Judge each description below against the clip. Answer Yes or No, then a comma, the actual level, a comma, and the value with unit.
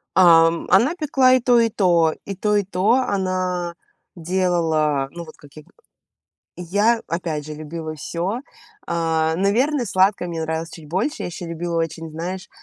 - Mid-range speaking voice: Yes, medium, 175 Hz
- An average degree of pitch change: Yes, average, 3.4 semitones